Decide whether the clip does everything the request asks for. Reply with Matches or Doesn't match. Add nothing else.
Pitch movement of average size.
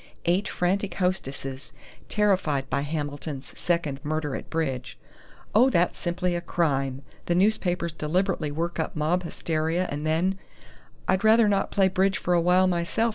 Matches